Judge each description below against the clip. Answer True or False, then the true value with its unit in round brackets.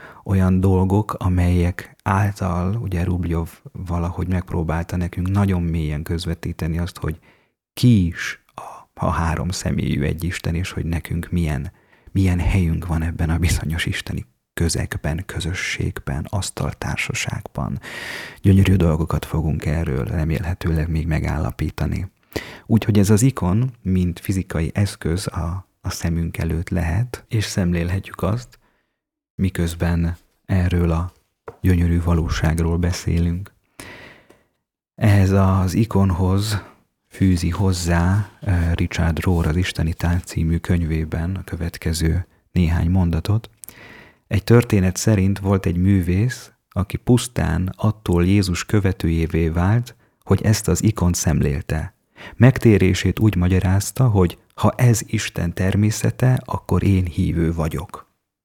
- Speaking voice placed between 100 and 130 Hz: False (90 Hz)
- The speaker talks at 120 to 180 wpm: False (110 wpm)